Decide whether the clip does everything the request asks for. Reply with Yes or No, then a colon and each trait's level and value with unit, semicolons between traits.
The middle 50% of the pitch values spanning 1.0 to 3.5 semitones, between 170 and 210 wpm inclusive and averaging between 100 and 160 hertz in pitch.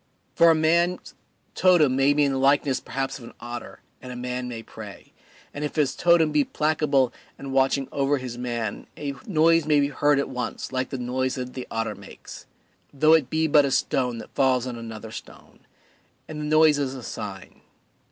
Yes: average, 3.2 semitones; average, 200 wpm; low, 135 Hz